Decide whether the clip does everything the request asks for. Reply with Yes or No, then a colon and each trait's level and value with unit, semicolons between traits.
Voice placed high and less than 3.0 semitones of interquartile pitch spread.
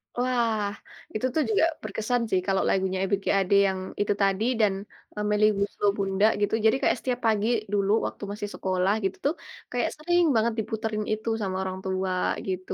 Yes: high, 205 Hz; narrow, 2.5 semitones